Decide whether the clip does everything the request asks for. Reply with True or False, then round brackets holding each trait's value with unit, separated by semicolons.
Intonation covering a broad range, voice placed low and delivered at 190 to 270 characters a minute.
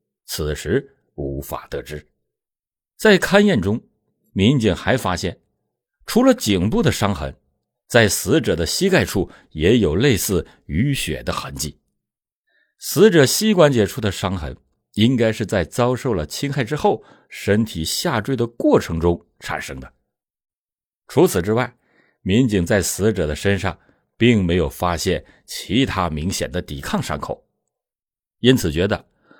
True (8.4 semitones; 100 Hz; 200 characters per minute)